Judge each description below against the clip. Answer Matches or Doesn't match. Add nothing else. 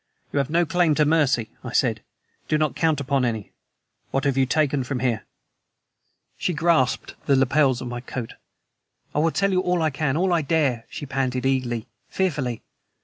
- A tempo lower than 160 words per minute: Doesn't match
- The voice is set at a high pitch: Doesn't match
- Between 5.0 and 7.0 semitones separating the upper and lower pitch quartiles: Doesn't match